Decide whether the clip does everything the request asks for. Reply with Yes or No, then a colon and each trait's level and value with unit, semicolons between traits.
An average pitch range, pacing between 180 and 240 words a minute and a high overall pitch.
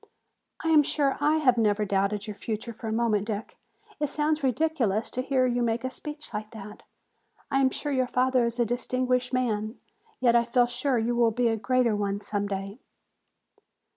Yes: average, 3.3 semitones; average, 195 wpm; high, 240 Hz